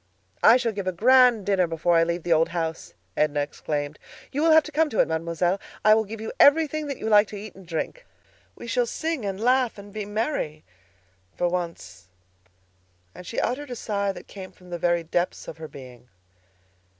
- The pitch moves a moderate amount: No, wide, 6.3 semitones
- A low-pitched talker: No, high, 195 Hz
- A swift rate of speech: Yes, fast, 210 wpm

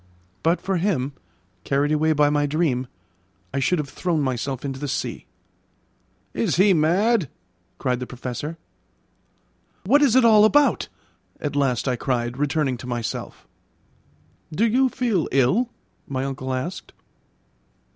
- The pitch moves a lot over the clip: Yes, wide, 6.2 semitones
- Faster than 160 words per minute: No, slow, 135 wpm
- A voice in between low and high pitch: Yes, medium, 145 Hz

